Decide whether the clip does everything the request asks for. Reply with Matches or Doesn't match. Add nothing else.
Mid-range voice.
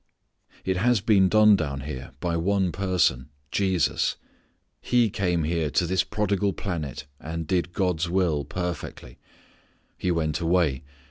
Doesn't match